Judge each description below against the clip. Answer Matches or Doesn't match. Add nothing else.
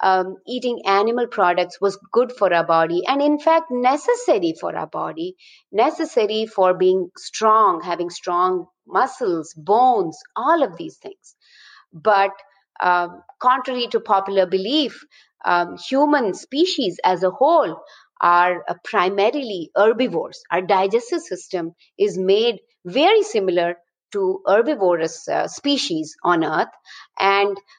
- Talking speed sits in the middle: Doesn't match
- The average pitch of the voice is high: Matches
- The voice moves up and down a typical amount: Doesn't match